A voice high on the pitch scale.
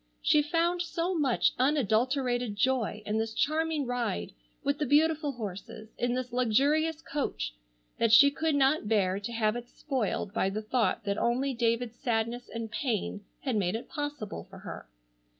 Yes: high, 245 Hz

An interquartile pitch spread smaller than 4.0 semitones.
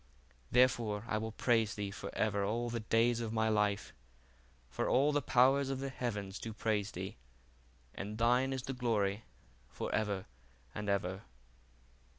Yes: average, 3.0 semitones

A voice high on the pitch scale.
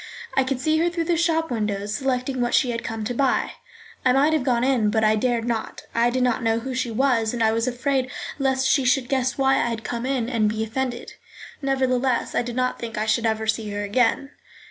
Yes: high, 245 Hz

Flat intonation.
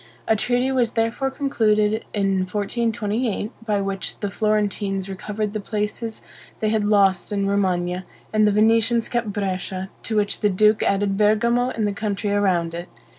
Yes: narrow, 2.1 semitones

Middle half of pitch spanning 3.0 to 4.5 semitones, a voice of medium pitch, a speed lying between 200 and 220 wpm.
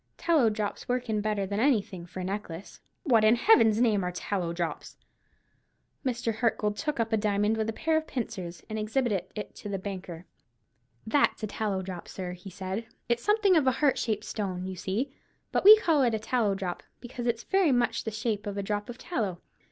No: average, 3.8 semitones; high, 215 Hz; fast, 205 wpm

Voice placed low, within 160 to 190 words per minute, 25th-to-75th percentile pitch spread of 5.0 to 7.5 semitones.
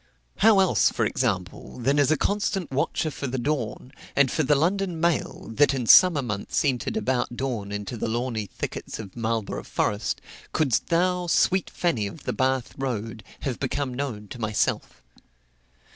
Yes: low, 130 Hz; average, 165 wpm; wide, 5.6 semitones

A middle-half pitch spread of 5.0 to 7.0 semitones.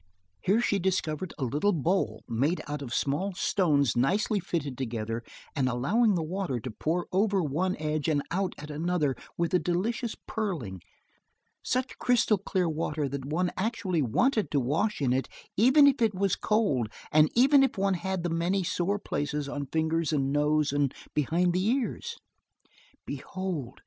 Yes: wide, 5.5 semitones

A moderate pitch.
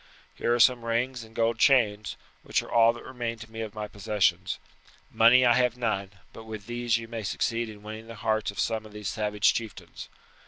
No: low, 115 Hz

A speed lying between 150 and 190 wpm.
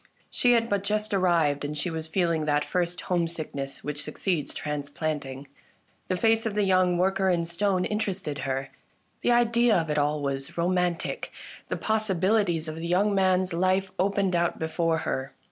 Yes: average, 170 wpm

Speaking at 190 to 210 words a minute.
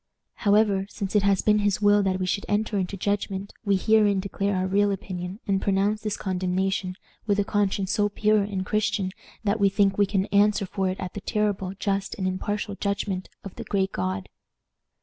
Yes: average, 195 wpm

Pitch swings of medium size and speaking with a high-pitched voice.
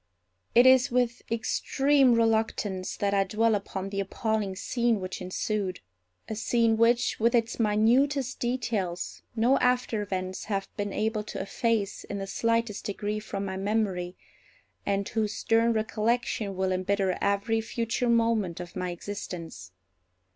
Yes: average, 3.0 semitones; high, 215 Hz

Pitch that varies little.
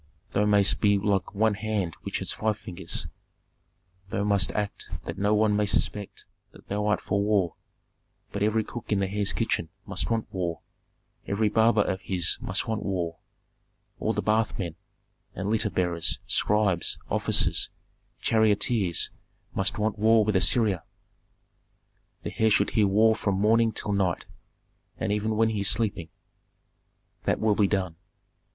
Yes: narrow, 2.1 semitones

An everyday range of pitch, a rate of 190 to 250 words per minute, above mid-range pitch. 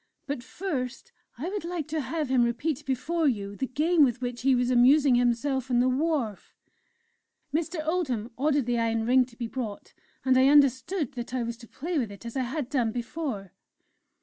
Yes: average, 4.0 semitones; average, 195 wpm; very high, 255 Hz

